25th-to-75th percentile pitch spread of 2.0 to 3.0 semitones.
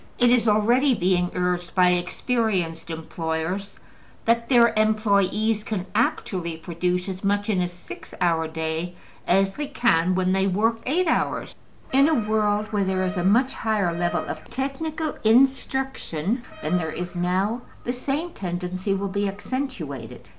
No: average, 4.7 semitones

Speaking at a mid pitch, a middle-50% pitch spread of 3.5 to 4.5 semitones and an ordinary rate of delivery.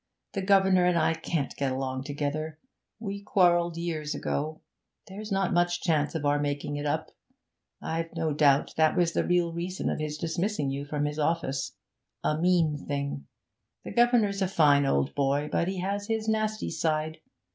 Yes: medium, 160 Hz; average, 4.0 semitones; average, 175 wpm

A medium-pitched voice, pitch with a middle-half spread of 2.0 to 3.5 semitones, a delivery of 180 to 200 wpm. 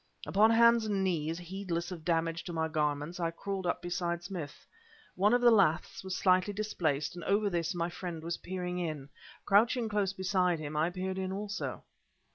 Yes: medium, 180 Hz; average, 3.0 semitones; average, 185 wpm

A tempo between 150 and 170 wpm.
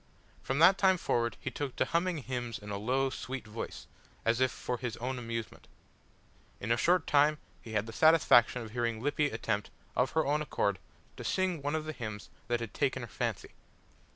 No: average, 200 wpm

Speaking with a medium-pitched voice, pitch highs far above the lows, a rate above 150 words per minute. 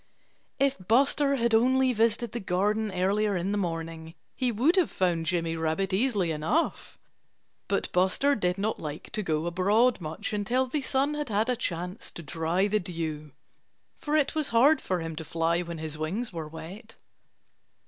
No: high, 195 Hz; wide, 6.6 semitones; average, 175 wpm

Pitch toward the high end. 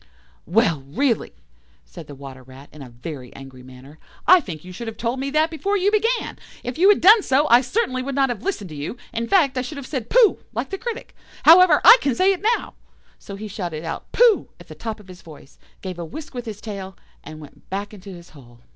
Yes: high, 225 Hz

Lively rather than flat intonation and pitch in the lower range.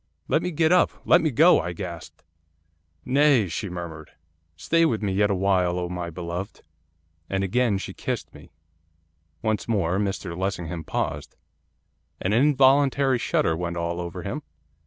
Yes: wide, 6.9 semitones; low, 100 Hz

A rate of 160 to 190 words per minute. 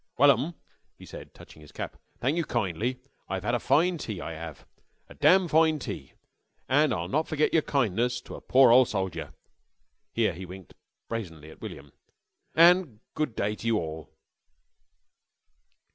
Yes: average, 165 wpm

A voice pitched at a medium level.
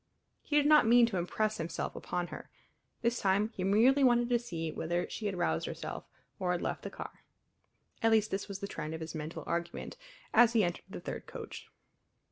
No: high, 200 Hz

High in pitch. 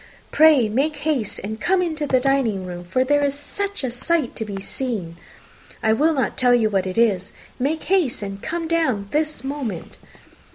Yes: very high, 260 Hz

